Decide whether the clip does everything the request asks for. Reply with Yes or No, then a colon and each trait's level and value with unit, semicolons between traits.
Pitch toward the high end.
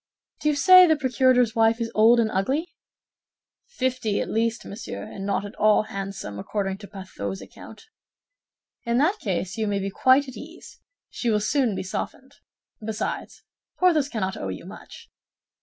Yes: high, 225 Hz